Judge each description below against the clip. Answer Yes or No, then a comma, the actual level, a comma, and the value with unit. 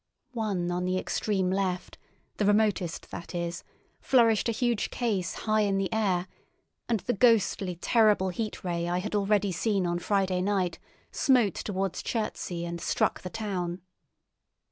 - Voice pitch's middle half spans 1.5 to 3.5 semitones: Yes, average, 3.1 semitones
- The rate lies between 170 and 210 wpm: No, average, 150 wpm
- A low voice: No, high, 195 Hz